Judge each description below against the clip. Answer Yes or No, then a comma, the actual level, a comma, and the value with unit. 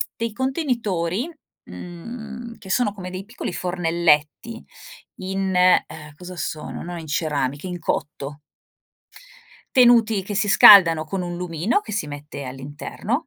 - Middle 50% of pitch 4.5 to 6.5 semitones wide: Yes, wide, 5.6 semitones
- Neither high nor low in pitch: Yes, medium, 180 Hz